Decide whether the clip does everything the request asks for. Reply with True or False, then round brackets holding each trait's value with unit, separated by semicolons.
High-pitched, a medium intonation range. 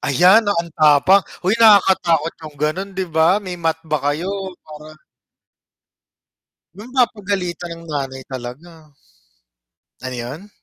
False (165 Hz; 4.2 semitones)